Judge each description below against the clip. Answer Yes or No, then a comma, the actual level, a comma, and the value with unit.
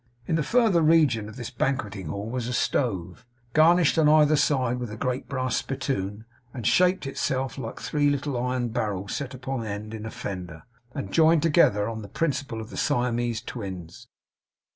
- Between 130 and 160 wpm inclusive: No, average, 185 wpm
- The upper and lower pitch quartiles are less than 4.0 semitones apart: No, average, 4.9 semitones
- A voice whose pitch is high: No, low, 125 Hz